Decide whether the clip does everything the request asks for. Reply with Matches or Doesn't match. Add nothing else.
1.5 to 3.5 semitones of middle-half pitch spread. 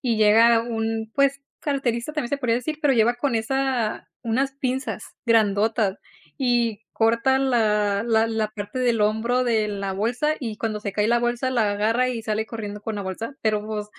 Matches